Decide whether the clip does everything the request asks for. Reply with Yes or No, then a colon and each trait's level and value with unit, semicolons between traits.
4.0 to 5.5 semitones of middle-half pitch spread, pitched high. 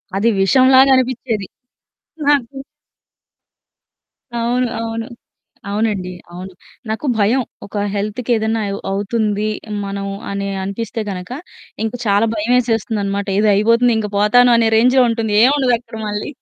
No: average, 3.3 semitones; high, 225 Hz